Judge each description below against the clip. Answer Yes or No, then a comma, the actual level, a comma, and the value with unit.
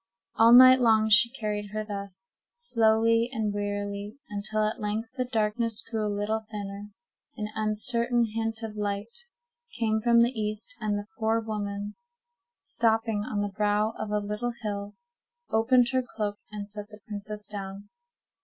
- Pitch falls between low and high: No, high, 215 Hz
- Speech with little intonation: Yes, narrow, 1.7 semitones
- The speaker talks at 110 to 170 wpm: Yes, average, 155 wpm